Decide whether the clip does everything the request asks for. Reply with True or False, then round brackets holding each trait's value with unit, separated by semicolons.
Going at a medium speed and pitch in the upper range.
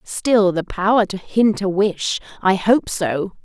True (175 wpm; 195 Hz)